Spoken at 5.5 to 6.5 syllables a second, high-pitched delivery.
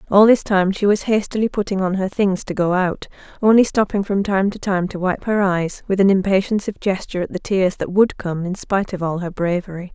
Yes: 5.7 syllables/s; high, 195 Hz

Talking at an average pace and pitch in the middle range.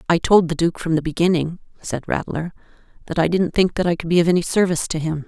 No: fast, 250 wpm; medium, 170 Hz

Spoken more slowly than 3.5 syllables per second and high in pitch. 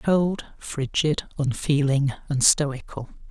No: 3.3 syllables/s; medium, 145 Hz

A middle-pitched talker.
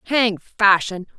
No: high, 205 Hz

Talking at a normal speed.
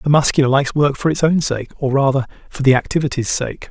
No: fast, 225 wpm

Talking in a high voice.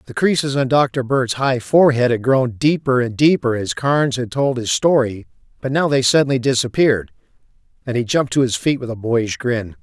No: low, 125 Hz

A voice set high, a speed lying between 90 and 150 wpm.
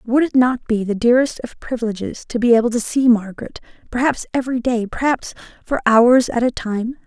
No: high, 240 Hz; average, 195 wpm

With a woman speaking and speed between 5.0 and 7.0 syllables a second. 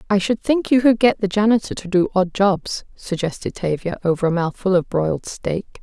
Yes: female; 5.3 syllables/s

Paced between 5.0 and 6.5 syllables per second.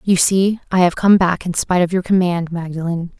Yes: 5.5 syllables/s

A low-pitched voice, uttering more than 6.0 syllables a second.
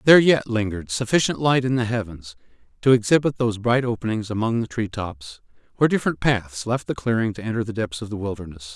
Yes: low, 110 Hz; 6.3 syllables/s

